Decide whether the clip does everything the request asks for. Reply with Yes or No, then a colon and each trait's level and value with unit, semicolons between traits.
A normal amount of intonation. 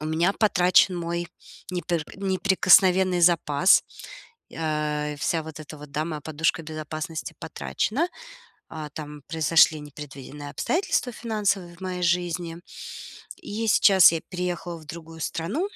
Yes: average, 3.1 semitones